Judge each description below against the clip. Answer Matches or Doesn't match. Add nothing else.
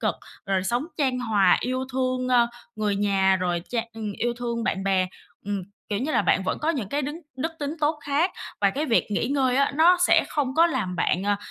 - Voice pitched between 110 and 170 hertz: Doesn't match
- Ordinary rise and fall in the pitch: Doesn't match